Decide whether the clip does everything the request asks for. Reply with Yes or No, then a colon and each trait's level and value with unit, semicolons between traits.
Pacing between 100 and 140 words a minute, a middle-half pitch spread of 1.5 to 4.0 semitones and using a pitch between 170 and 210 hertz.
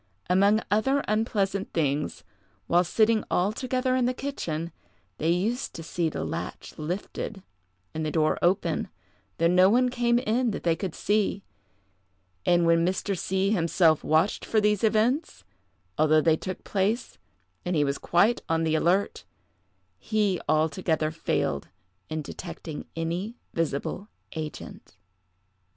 No: slow, 135 wpm; average, 4.9 semitones; medium, 185 Hz